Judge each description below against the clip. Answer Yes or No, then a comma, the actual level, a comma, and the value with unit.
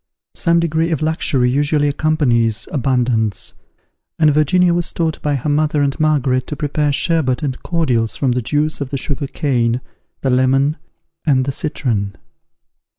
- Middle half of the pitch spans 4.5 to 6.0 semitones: No, average, 3.3 semitones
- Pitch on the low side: No, medium, 145 Hz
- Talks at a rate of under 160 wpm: Yes, average, 150 wpm